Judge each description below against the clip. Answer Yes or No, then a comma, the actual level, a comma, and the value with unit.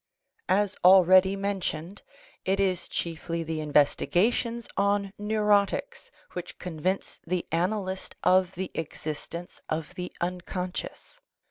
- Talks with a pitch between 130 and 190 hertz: Yes, medium, 185 Hz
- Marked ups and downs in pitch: No, average, 2.8 semitones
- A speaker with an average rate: No, slow, 105 wpm